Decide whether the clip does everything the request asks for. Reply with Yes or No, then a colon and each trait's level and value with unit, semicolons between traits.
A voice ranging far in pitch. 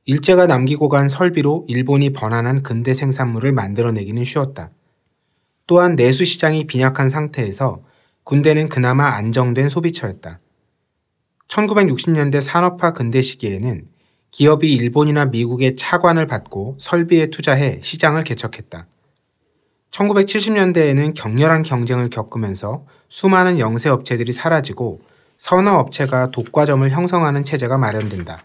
No: average, 4.5 semitones